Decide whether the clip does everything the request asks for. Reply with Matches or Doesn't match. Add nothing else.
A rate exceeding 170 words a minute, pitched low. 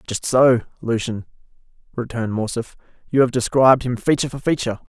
Doesn't match